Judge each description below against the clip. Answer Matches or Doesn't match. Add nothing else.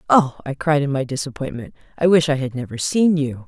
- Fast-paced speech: Matches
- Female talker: Matches